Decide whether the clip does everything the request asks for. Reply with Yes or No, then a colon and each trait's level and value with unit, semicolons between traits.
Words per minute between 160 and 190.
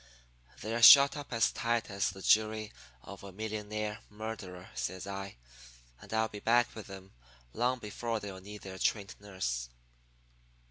No: average, 150 wpm